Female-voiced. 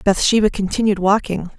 Yes: female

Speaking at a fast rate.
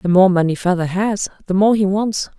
Yes: fast, 225 wpm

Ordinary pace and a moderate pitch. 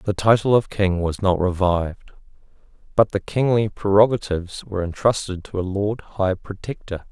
No: average, 150 wpm; low, 100 Hz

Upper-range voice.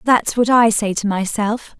Yes: high, 220 Hz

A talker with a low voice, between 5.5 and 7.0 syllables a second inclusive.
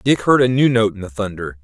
Yes: low, 110 Hz; 6.0 syllables/s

